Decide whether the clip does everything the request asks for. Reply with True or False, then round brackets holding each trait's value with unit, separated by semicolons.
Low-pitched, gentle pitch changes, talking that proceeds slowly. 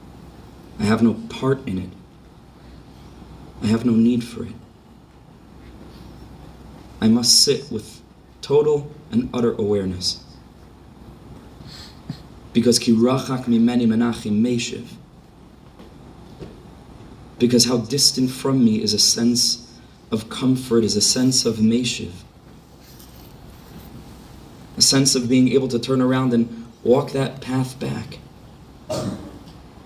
True (120 Hz; 2.2 semitones; 110 wpm)